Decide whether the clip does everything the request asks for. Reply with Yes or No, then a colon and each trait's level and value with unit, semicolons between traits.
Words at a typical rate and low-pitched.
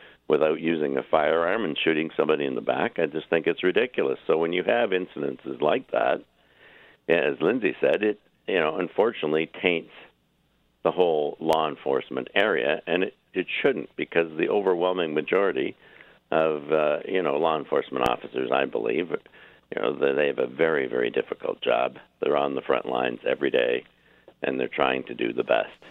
No: average, 175 wpm; very high, 370 Hz